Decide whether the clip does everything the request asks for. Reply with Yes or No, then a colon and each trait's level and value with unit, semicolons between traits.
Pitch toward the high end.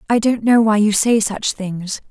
Yes: high, 215 Hz